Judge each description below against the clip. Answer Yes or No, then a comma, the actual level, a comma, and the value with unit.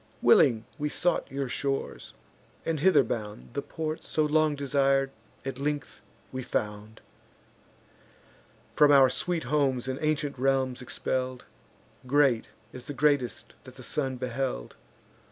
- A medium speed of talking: No, slow, 130 wpm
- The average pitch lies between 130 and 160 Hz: Yes, low, 135 Hz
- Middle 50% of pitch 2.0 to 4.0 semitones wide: Yes, narrow, 2.6 semitones